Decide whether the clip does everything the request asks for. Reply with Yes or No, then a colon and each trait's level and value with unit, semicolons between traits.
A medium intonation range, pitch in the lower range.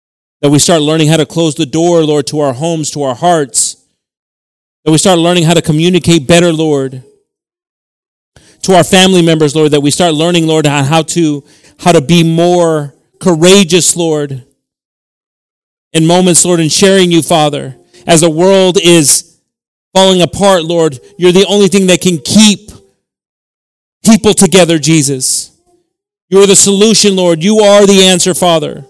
No: average, 3.6 semitones; medium, 170 Hz